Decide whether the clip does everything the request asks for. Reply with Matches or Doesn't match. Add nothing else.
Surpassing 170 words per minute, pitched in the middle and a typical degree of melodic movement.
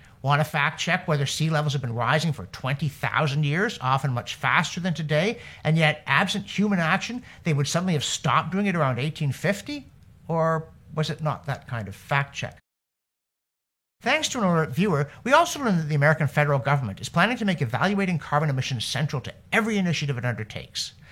Matches